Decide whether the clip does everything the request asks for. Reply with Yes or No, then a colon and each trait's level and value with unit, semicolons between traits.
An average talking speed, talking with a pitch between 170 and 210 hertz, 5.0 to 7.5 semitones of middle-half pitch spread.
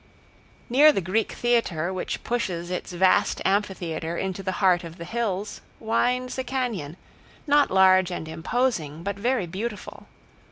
Yes: average, 145 wpm; high, 190 Hz; average, 5.3 semitones